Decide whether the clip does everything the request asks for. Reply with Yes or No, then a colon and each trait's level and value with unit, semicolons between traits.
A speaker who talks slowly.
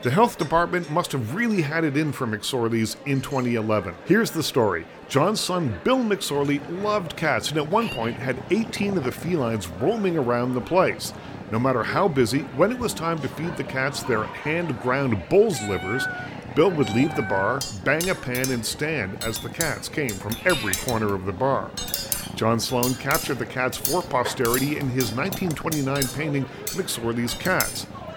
No: average, 180 wpm